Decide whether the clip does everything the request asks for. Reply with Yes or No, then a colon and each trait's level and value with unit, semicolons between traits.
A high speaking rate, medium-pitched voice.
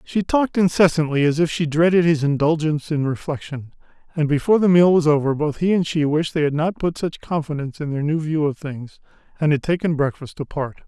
Yes: fast, 215 wpm; medium, 155 Hz